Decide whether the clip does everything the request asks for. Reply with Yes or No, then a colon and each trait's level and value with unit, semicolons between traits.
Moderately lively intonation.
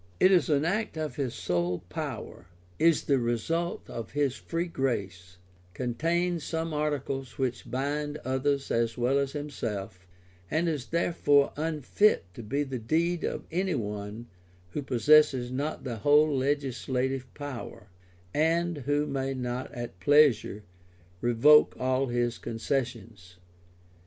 Yes: average, 4.1 semitones